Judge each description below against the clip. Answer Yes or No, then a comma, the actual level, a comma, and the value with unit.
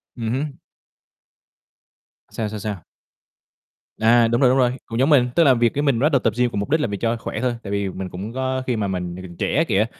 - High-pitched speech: No, low, 115 Hz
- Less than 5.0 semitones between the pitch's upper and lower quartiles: Yes, average, 4.3 semitones